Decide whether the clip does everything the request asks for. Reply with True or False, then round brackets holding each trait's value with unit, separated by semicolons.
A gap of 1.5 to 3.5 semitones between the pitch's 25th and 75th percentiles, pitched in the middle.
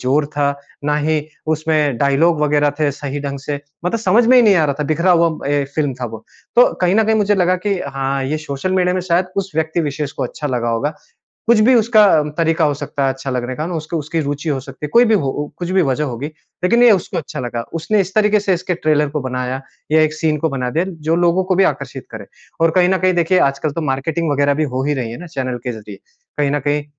False (4.2 semitones; 155 Hz)